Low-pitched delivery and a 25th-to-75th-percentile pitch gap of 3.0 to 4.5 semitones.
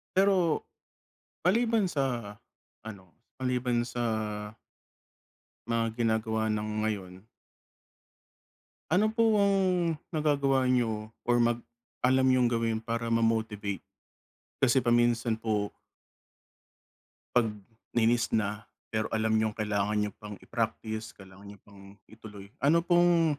Yes: low, 115 Hz; average, 3.3 semitones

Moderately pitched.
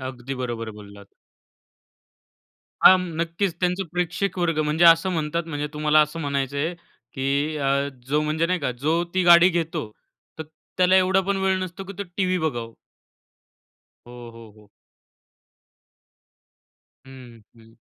Yes: medium, 160 Hz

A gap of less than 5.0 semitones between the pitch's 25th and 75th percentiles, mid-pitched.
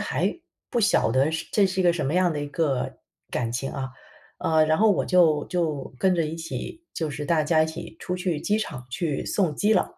Yes: average, 3.6 semitones; medium, 160 Hz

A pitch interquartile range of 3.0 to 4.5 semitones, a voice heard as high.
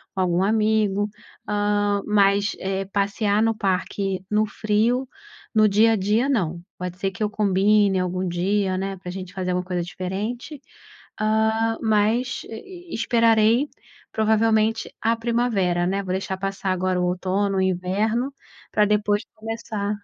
No: narrow, 2.6 semitones; high, 205 Hz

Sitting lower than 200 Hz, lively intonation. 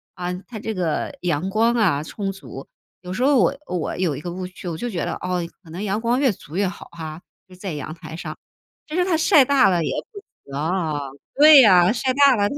Yes: medium, 185 Hz; wide, 6.3 semitones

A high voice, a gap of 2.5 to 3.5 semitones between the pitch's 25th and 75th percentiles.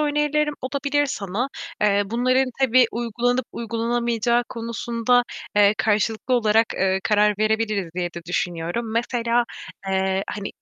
Yes: high, 230 Hz; average, 2.9 semitones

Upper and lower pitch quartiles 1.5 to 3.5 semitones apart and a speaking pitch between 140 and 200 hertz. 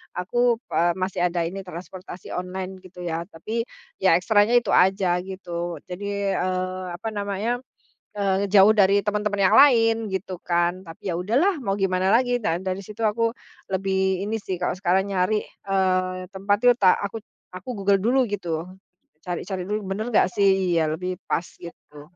Yes: narrow, 2.4 semitones; high, 190 Hz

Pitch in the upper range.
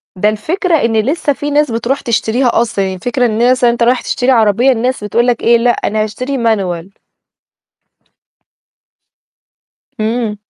Yes: high, 235 Hz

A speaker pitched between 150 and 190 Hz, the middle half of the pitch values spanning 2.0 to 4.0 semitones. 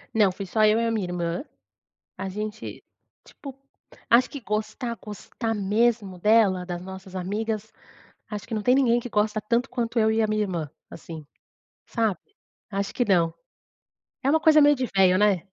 No: high, 215 Hz; average, 3.5 semitones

